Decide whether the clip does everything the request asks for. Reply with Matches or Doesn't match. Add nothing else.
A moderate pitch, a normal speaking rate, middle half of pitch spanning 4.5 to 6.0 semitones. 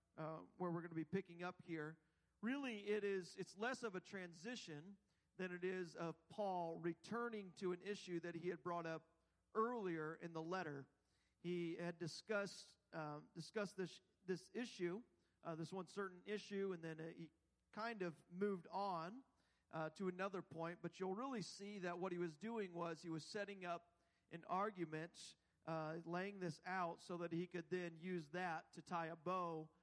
Doesn't match